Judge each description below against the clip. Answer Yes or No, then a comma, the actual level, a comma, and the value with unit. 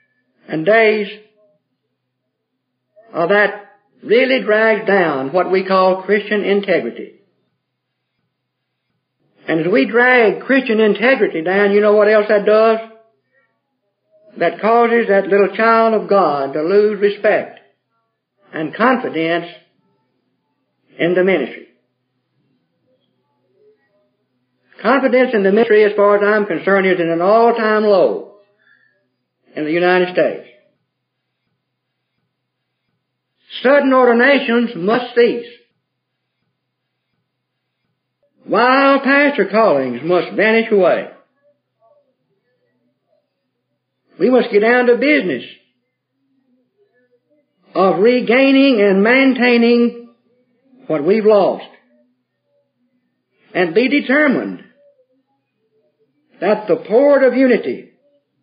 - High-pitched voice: Yes, high, 220 Hz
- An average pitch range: Yes, average, 4.4 semitones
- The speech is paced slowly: Yes, slow, 90 wpm